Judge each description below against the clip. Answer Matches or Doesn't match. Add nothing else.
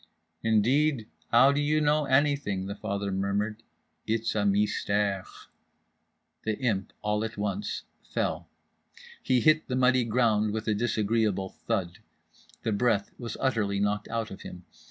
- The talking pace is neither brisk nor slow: Matches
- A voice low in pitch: Matches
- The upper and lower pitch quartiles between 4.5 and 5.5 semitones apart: Doesn't match